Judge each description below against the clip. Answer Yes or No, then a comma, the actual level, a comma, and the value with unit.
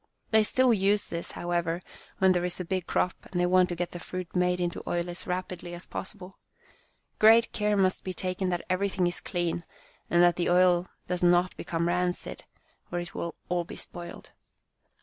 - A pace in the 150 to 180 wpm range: No, average, 190 wpm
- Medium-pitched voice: Yes, medium, 180 Hz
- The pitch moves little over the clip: Yes, narrow, 1.2 semitones